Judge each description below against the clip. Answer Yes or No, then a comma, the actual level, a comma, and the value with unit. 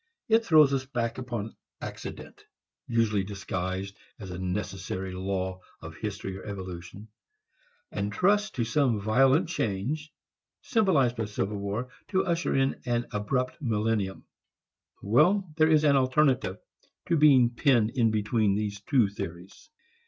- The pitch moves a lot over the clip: Yes, wide, 5.8 semitones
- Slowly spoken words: Yes, slow, 130 wpm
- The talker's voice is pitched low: Yes, low, 115 Hz